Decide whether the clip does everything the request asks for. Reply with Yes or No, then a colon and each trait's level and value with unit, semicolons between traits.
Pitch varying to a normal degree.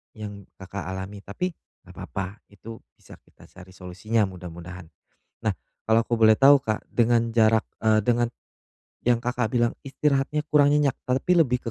Yes: average, 3.9 semitones